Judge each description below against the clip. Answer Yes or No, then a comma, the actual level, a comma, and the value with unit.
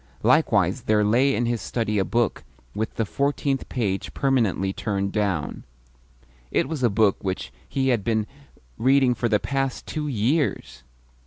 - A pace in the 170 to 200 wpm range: No, average, 155 wpm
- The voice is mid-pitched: No, low, 115 Hz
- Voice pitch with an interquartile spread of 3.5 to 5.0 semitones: Yes, average, 4.4 semitones